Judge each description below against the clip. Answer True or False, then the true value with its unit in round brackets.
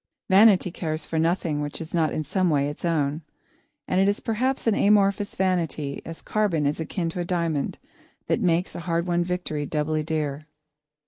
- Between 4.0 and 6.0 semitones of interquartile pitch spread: False (3.3 semitones)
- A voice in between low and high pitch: True (170 Hz)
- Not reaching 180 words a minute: False (185 wpm)